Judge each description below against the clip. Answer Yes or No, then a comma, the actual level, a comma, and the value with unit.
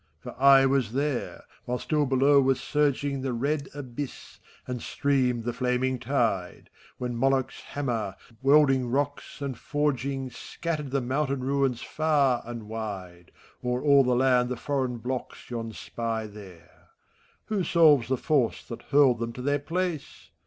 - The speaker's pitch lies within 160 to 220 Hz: No, low, 130 Hz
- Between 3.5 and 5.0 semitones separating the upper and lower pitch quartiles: No, average, 2.8 semitones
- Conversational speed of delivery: Yes, average, 150 wpm